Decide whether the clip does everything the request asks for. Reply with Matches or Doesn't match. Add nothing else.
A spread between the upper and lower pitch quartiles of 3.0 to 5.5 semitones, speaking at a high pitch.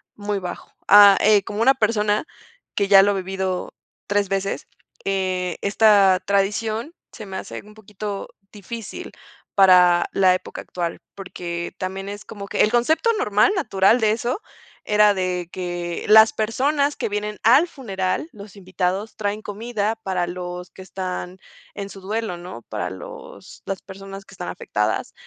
Doesn't match